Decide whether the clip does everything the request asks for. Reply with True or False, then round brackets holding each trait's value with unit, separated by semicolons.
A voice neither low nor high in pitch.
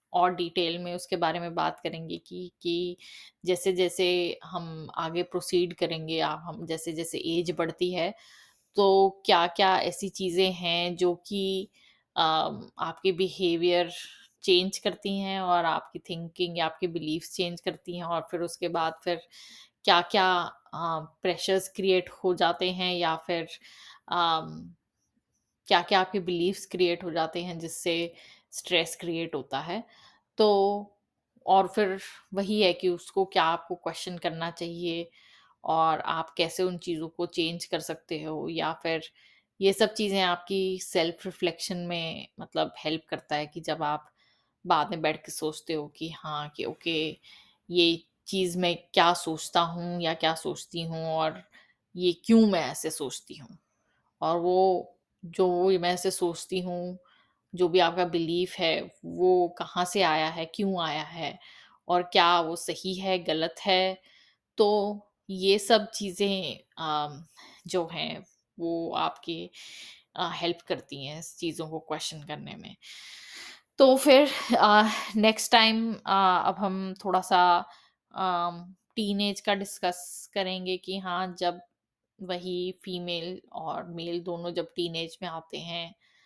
True (175 Hz)